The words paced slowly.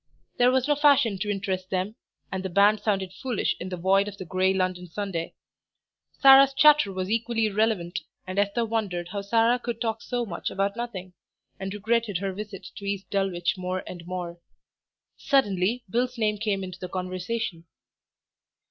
No: average, 170 wpm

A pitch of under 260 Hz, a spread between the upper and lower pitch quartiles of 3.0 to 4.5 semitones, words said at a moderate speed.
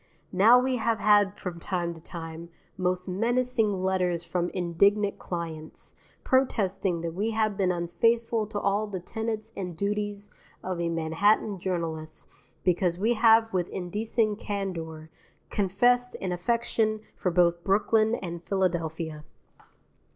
No: high, 190 Hz; average, 4.0 semitones; slow, 130 wpm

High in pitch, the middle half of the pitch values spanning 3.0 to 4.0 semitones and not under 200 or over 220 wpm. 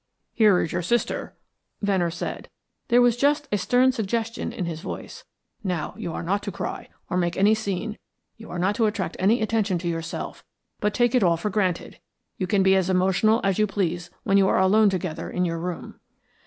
Yes: high, 195 Hz; average, 3.5 semitones; fast, 205 wpm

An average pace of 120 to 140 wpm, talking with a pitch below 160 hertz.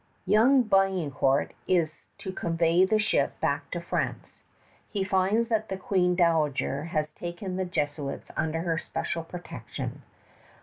No: slow, 135 wpm; medium, 175 Hz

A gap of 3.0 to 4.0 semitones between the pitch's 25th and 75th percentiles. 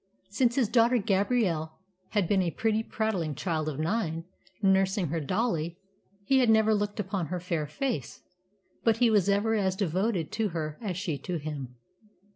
No: average, 5.1 semitones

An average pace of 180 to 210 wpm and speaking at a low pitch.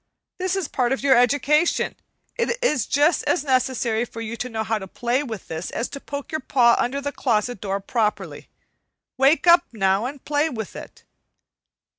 No: average, 190 wpm; very high, 255 Hz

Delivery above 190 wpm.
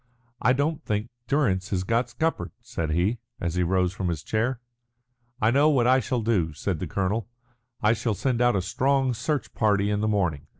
Yes: average, 200 wpm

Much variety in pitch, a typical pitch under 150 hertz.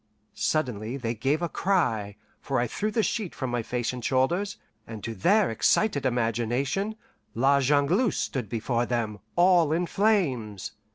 Yes: wide, 7.1 semitones; low, 135 Hz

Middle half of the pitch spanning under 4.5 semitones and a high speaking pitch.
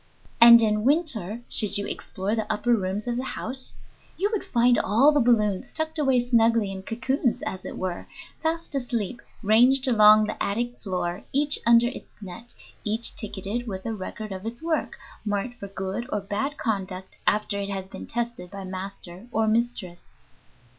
Yes: average, 3.6 semitones; high, 225 Hz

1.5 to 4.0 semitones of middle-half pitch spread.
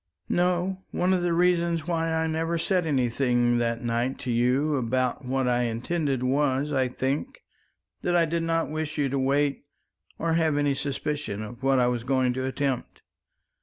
No: average, 4.5 semitones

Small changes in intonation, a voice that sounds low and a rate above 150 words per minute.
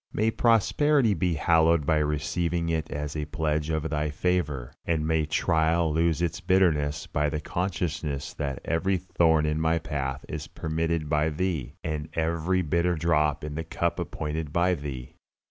Yes: narrow, 2.2 semitones; very low, 80 Hz; average, 160 wpm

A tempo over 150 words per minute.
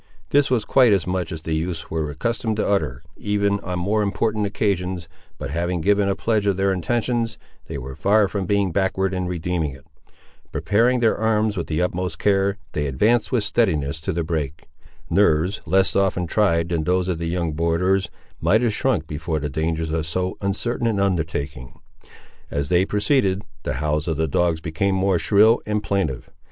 Yes: average, 185 wpm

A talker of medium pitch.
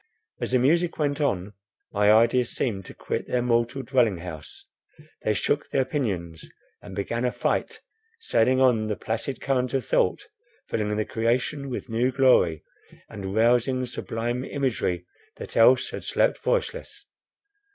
No: low, 120 Hz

